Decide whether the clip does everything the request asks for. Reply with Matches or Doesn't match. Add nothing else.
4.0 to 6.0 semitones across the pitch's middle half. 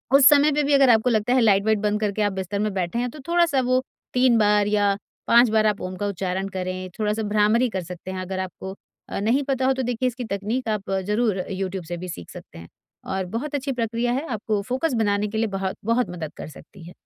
Matches